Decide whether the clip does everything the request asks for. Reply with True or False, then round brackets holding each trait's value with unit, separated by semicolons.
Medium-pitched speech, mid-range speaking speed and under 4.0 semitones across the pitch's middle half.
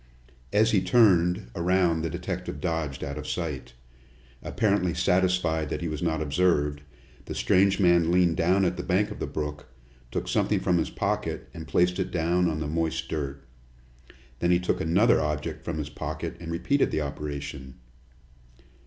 False (85 Hz; 170 wpm; 3.0 semitones)